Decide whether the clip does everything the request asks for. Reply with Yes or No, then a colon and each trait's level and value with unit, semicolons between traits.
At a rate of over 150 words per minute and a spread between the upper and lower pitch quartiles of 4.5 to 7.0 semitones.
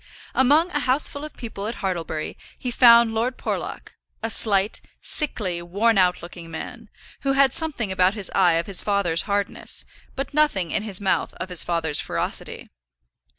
Yes: average, 165 wpm; wide, 5.5 semitones